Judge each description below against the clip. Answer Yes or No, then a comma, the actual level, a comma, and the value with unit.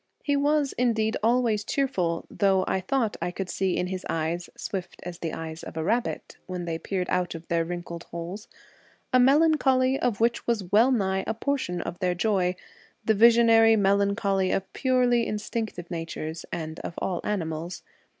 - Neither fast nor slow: Yes, average, 170 wpm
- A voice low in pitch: No, high, 195 Hz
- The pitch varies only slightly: No, average, 5.0 semitones